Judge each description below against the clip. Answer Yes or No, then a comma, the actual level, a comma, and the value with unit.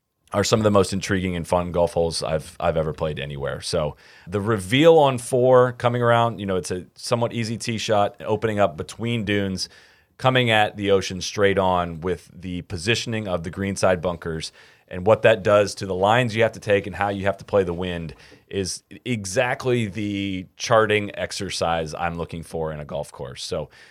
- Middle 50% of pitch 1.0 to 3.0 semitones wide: No, average, 4.1 semitones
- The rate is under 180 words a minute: No, average, 200 wpm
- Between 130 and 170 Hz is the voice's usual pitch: No, low, 100 Hz